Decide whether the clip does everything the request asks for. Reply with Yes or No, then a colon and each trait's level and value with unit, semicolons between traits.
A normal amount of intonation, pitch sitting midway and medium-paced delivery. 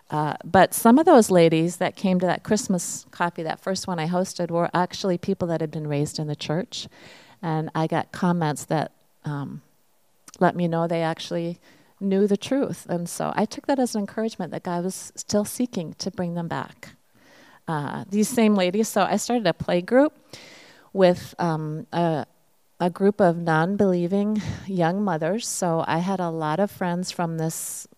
Yes: average, 3.5 semitones; medium, 180 Hz; average, 185 wpm